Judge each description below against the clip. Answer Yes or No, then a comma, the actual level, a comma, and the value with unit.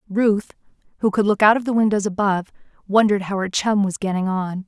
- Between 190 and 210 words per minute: Yes, fast, 205 wpm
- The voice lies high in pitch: Yes, high, 200 Hz